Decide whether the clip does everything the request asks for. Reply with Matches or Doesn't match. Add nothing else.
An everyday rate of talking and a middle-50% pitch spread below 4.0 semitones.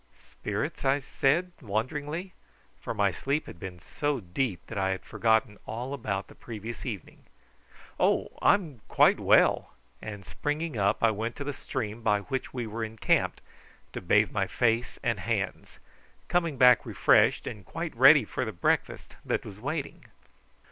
Doesn't match